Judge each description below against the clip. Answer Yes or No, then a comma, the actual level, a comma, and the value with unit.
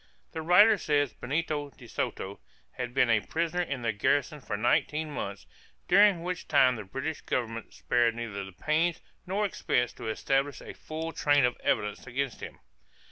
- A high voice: No, medium, 140 Hz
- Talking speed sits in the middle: Yes, average, 170 wpm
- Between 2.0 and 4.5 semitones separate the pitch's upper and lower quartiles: No, wide, 5.4 semitones